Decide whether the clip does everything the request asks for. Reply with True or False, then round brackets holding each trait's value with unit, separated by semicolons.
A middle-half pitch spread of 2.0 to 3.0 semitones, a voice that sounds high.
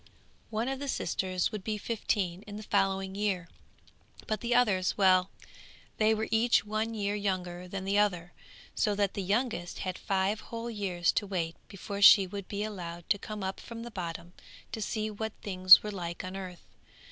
True (2.7 semitones; 200 Hz)